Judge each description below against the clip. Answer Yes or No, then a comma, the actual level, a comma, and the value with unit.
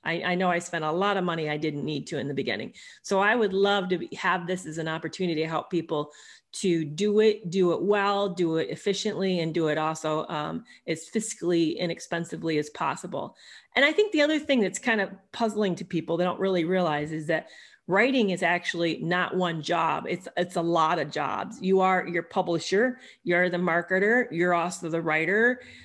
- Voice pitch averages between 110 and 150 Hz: No, medium, 175 Hz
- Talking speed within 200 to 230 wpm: Yes, fast, 205 wpm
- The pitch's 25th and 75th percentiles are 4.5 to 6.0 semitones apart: No, average, 3.3 semitones